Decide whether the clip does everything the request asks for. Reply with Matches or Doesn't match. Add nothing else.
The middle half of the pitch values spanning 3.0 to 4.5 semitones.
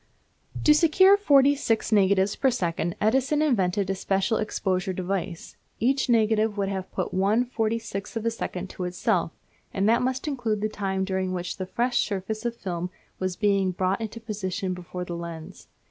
Matches